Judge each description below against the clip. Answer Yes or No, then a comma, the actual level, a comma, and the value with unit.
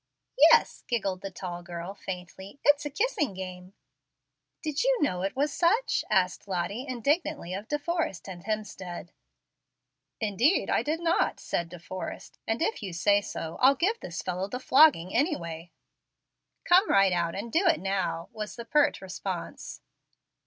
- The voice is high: Yes, high, 205 Hz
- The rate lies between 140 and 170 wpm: Yes, average, 160 wpm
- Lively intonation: Yes, wide, 8.4 semitones